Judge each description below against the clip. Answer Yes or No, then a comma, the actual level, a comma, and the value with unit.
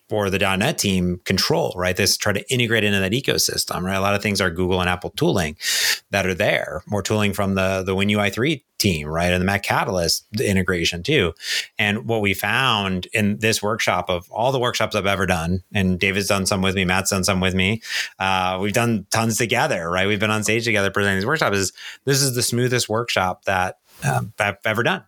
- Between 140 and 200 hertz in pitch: No, low, 100 Hz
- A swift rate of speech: Yes, fast, 225 wpm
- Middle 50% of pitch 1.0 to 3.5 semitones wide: Yes, narrow, 2.6 semitones